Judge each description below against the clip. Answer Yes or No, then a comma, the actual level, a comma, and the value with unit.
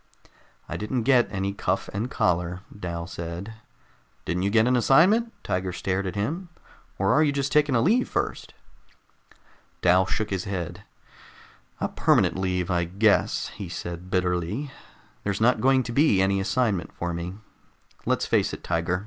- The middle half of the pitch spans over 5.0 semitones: Yes, wide, 5.5 semitones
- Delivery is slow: No, average, 160 wpm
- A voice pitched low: Yes, low, 100 Hz